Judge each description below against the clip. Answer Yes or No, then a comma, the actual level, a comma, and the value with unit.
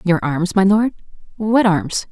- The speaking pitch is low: No, high, 190 Hz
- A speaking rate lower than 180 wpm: Yes, average, 140 wpm